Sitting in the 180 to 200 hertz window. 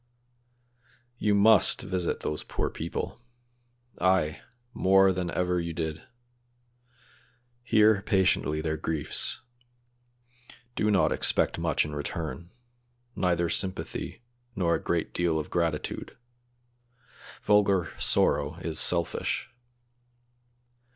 No: very low, 90 Hz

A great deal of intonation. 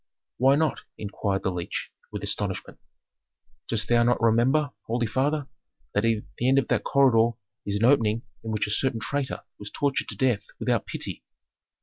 No: average, 3.8 semitones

